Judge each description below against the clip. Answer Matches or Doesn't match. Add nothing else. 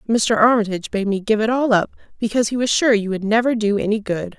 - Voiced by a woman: Matches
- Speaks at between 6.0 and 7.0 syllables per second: Matches